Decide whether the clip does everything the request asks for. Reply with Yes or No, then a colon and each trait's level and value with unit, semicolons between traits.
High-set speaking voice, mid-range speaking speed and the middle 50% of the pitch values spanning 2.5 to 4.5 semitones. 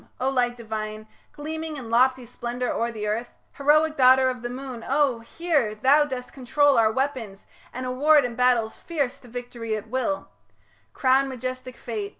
Yes: very high, 255 Hz; average, 165 wpm; average, 2.8 semitones